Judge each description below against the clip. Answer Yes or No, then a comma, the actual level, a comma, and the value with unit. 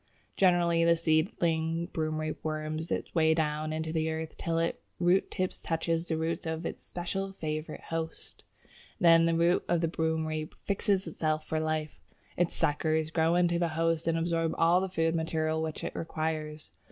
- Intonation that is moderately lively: No, narrow, 1.2 semitones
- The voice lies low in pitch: No, medium, 160 Hz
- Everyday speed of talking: Yes, average, 170 wpm